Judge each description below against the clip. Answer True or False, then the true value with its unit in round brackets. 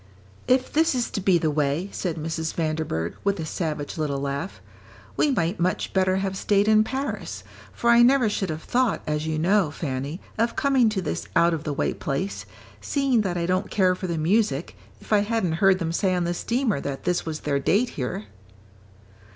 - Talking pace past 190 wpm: True (200 wpm)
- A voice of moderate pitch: True (180 Hz)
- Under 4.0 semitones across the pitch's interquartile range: False (5.3 semitones)